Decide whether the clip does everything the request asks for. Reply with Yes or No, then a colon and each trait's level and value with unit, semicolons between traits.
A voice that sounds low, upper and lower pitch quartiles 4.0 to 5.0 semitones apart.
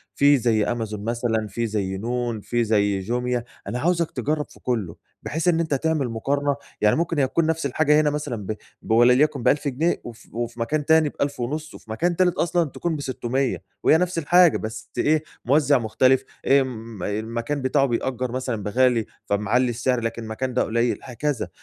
Yes: low, 125 Hz; average, 4.4 semitones